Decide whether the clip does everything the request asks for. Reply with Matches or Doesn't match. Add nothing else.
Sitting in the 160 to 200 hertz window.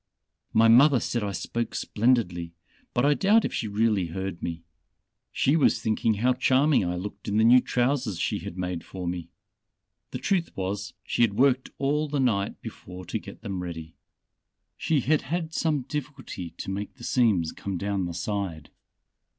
Doesn't match